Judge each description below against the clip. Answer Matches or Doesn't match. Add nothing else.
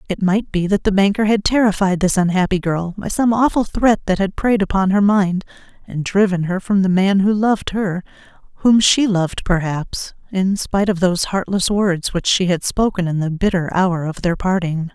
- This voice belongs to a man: Doesn't match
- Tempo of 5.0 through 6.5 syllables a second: Matches